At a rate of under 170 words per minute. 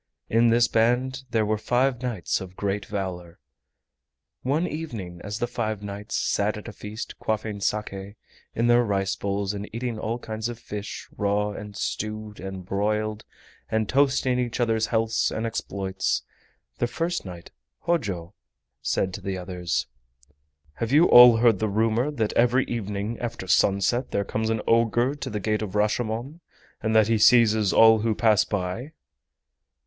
Yes: average, 160 wpm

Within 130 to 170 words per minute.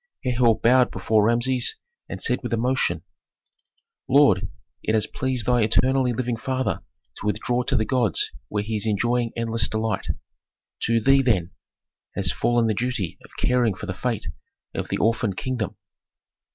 Yes: average, 155 wpm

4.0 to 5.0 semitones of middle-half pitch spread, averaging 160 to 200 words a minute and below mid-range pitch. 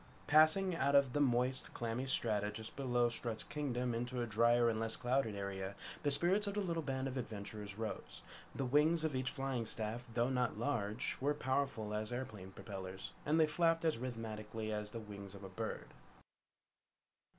Yes: average, 4.3 semitones; average, 180 wpm; low, 120 Hz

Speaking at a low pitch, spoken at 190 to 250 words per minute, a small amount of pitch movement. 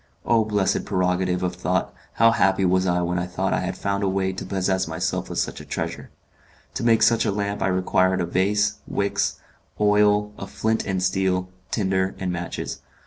Yes: very low, 95 Hz; average, 195 wpm; narrow, 1.9 semitones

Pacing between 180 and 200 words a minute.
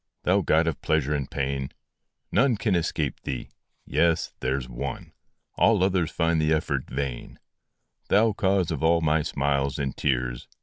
No: average, 165 wpm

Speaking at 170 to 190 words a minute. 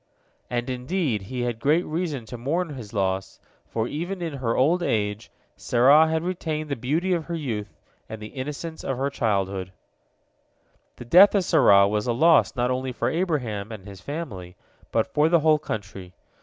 Yes: average, 180 wpm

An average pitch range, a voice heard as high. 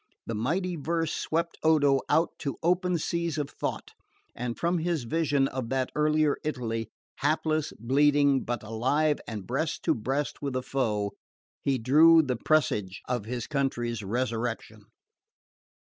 No: average, 4.6 semitones; medium, 140 Hz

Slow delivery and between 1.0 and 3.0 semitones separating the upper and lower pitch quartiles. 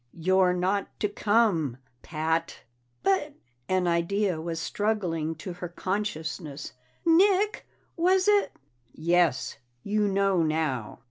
No: slow, 120 wpm; average, 4.5 semitones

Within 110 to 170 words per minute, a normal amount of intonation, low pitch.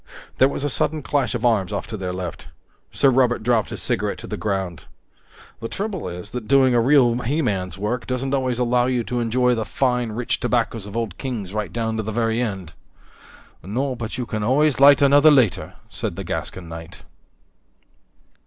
No: average, 195 wpm; average, 3.7 semitones; low, 120 Hz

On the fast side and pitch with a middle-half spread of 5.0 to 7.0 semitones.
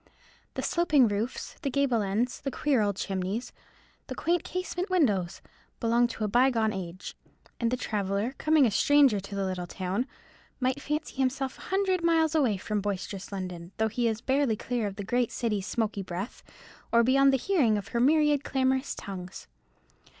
No: average, 175 wpm; wide, 5.4 semitones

